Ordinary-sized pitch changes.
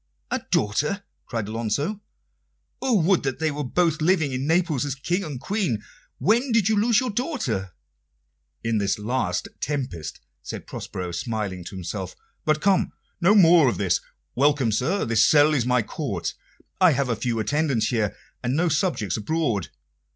No: wide, 7.9 semitones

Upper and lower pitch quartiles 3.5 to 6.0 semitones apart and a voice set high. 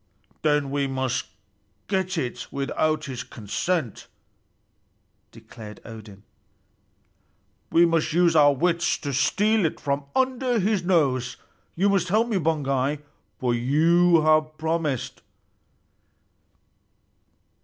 No: average, 4.6 semitones; medium, 155 Hz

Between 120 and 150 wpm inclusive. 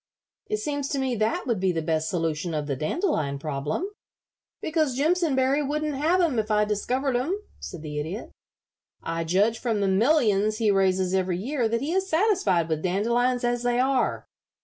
No: average, 180 wpm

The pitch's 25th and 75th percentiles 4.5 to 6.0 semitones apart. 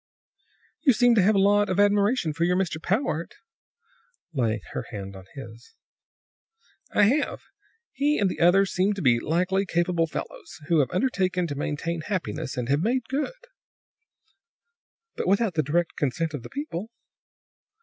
Yes: average, 5.0 semitones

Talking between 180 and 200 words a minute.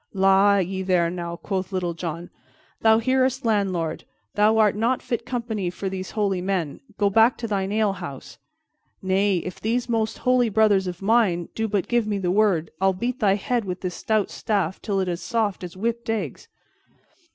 Yes: average, 185 wpm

